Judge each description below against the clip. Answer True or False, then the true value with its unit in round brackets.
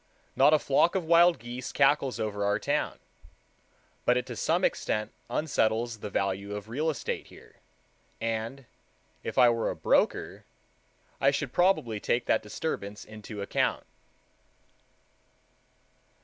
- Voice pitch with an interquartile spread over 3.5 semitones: True (4.9 semitones)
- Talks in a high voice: False (120 Hz)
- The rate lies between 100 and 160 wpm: True (135 wpm)